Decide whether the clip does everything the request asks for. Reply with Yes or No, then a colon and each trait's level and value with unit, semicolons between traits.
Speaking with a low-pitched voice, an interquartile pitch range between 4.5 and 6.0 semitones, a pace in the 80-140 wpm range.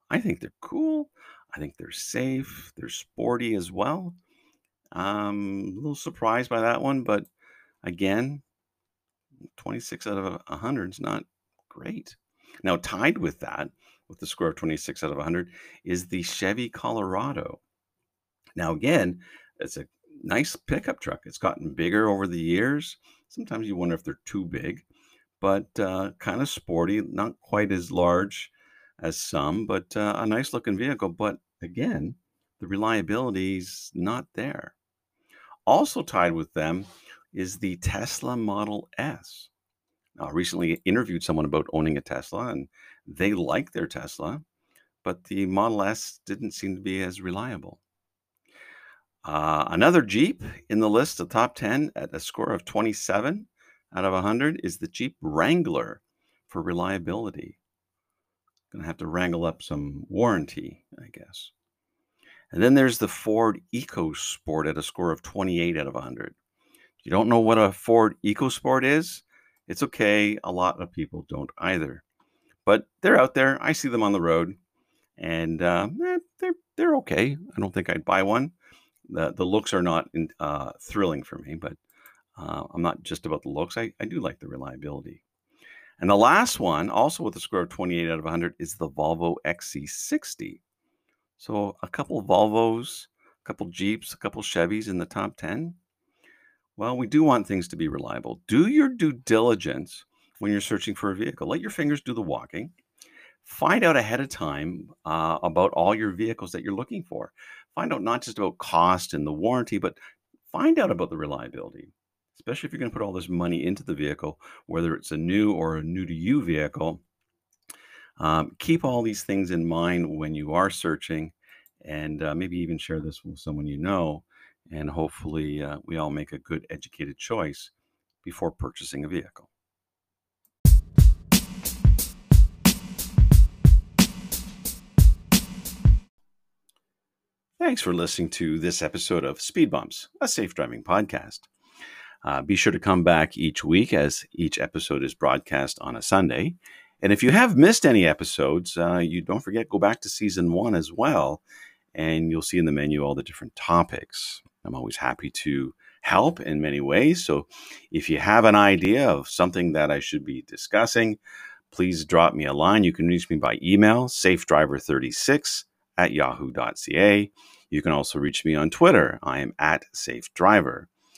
No: very low, 95 Hz; average, 5.3 semitones; average, 170 wpm